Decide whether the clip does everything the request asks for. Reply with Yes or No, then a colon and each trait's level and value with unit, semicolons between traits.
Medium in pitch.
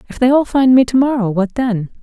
No: high, 240 Hz